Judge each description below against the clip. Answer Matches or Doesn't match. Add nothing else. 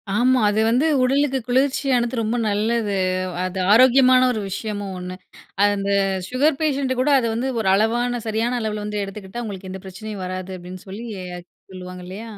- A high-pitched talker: Matches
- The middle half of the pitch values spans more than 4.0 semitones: Matches